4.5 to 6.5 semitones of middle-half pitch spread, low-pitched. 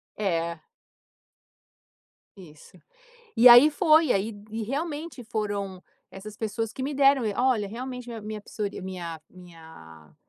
No: average, 5.3 semitones; high, 215 Hz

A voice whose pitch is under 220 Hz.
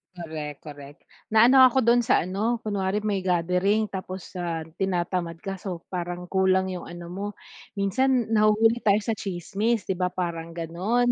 Yes: high, 190 Hz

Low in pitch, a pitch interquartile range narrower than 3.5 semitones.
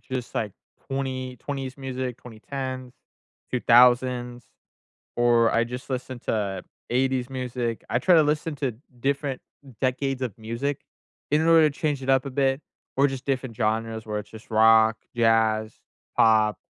Yes: low, 125 Hz; average, 2.9 semitones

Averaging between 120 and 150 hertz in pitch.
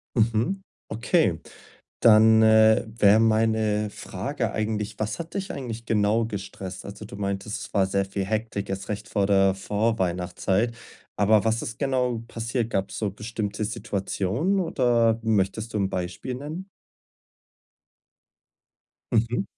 No: low, 110 Hz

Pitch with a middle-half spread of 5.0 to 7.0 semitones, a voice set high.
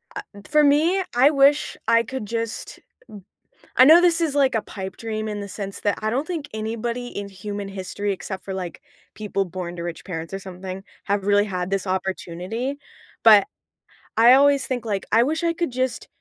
Yes: wide, 5.4 semitones; high, 215 Hz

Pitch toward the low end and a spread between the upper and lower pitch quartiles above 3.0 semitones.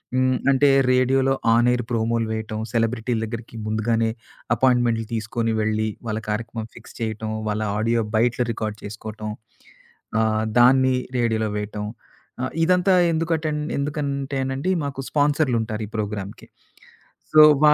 Yes: low, 115 Hz; average, 3.4 semitones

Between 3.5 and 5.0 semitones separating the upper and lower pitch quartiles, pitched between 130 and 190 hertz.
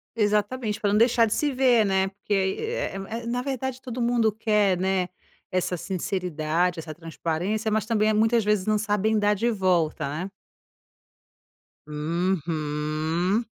No: average, 4.1 semitones; high, 205 Hz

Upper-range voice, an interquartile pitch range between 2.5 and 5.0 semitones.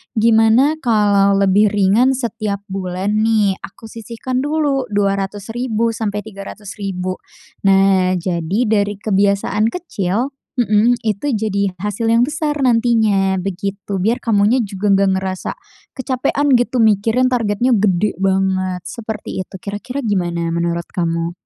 Yes: high, 205 Hz; average, 3.1 semitones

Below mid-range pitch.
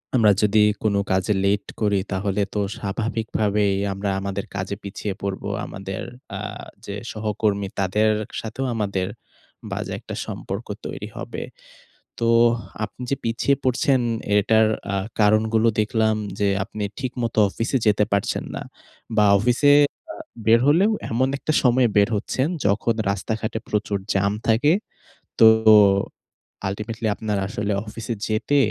Yes: low, 110 Hz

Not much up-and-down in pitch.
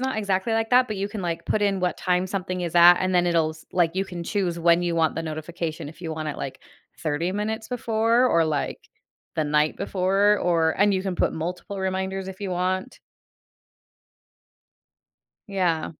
No: average, 3.0 semitones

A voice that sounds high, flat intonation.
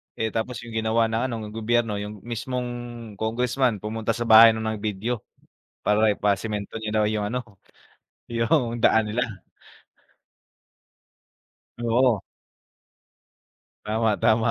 No: low, 110 Hz; narrow, 1.7 semitones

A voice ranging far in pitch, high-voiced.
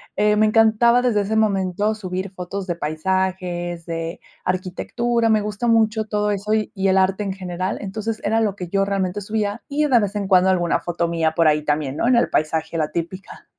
No: average, 3.4 semitones; high, 195 Hz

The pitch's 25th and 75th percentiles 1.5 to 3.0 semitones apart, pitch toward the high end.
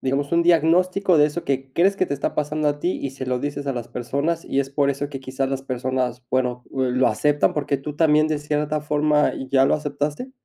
No: narrow, 2.4 semitones; medium, 145 Hz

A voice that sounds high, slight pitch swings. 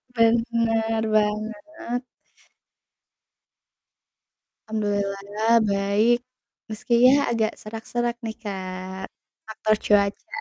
Yes: high, 220 Hz; narrow, 2.1 semitones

